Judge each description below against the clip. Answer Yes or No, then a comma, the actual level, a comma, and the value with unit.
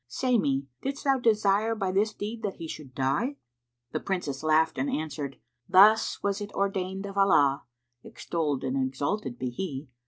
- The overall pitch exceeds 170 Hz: Yes, high, 190 Hz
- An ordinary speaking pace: Yes, average, 165 wpm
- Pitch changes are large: Yes, wide, 7.0 semitones